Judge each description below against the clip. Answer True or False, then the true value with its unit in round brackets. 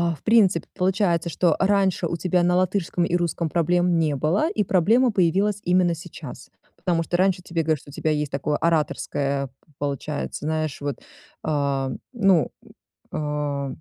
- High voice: False (170 Hz)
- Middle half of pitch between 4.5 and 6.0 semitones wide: False (3.6 semitones)